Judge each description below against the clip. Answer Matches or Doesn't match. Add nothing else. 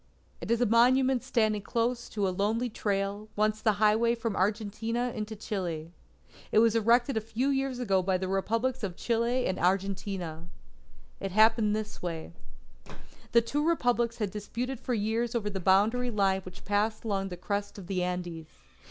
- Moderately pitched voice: Doesn't match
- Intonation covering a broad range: Doesn't match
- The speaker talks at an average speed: Matches